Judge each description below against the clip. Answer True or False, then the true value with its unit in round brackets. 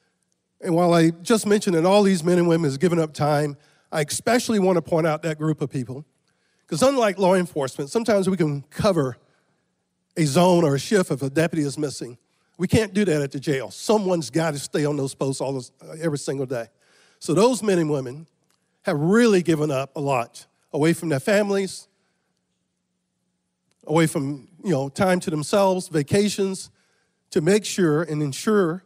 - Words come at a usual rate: True (185 wpm)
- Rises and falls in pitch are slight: False (4.5 semitones)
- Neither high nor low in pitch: True (160 Hz)